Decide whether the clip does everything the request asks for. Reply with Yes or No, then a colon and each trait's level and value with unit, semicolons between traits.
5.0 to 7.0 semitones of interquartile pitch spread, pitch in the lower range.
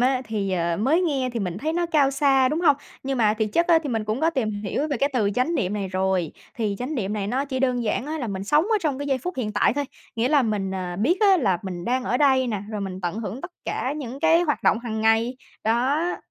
No: wide, 5.5 semitones; very high, 250 Hz